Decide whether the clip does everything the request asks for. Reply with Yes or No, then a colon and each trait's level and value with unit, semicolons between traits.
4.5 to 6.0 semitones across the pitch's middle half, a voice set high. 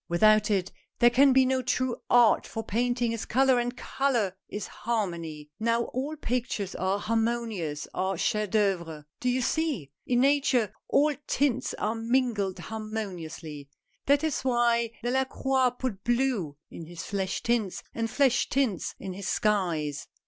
Yes: average, 4.9 semitones; high, 225 Hz